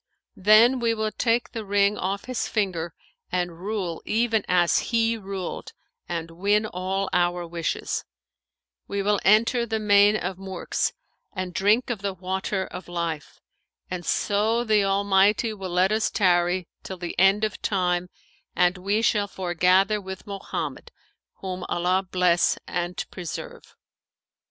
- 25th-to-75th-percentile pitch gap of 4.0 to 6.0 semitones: No, average, 2.8 semitones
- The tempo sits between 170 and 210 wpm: No, average, 140 wpm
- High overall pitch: Yes, high, 195 Hz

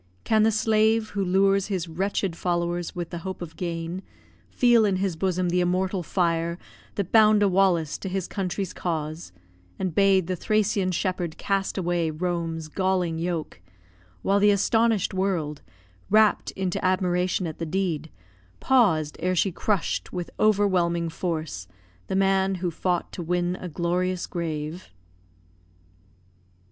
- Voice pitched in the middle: Yes, medium, 180 Hz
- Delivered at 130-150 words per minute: Yes, average, 145 wpm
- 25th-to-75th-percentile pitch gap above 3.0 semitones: No, narrow, 2.4 semitones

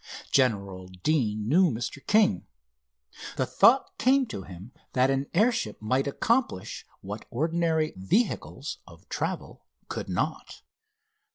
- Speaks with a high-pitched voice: No, low, 135 Hz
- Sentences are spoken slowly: Yes, slow, 115 wpm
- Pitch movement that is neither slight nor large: No, wide, 8.9 semitones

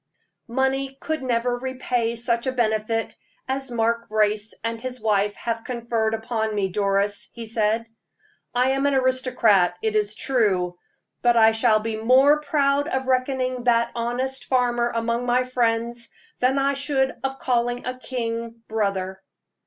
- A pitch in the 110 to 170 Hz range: No, high, 235 Hz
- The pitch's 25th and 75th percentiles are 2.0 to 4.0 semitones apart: Yes, narrow, 2.6 semitones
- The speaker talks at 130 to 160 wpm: Yes, average, 150 wpm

